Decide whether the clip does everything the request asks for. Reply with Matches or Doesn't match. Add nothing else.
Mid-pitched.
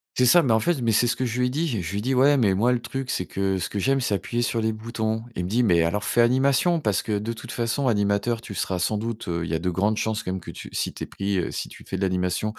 Doesn't match